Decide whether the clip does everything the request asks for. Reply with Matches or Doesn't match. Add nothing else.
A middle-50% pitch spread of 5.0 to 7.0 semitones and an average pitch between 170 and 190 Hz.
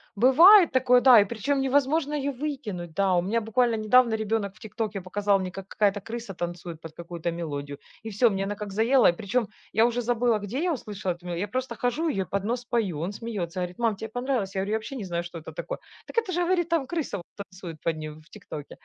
Doesn't match